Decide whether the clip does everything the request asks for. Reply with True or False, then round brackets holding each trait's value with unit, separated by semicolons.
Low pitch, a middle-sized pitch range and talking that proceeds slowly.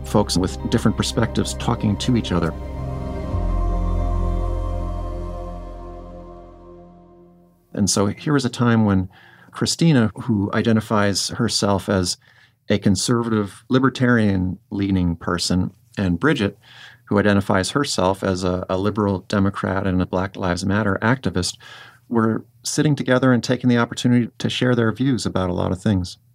True (100 Hz; 4.7 semitones; 130 wpm)